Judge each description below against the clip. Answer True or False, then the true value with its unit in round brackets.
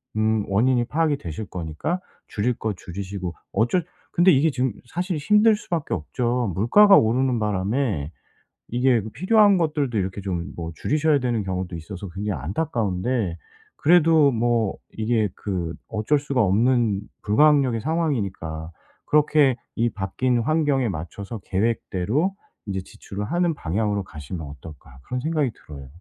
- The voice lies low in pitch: True (115 Hz)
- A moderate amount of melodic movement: False (7.1 semitones)